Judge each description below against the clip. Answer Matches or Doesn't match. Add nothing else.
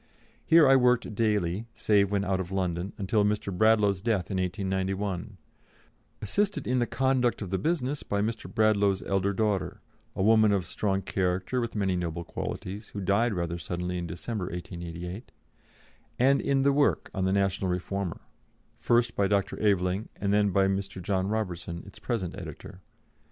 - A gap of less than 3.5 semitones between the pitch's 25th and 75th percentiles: Matches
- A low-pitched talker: Matches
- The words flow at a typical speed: Matches